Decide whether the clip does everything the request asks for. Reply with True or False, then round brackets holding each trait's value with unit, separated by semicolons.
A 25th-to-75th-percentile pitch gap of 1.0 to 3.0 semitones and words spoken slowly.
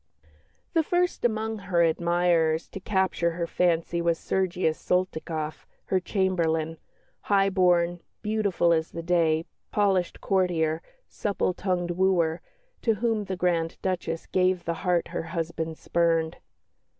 True (2.4 semitones; 125 wpm)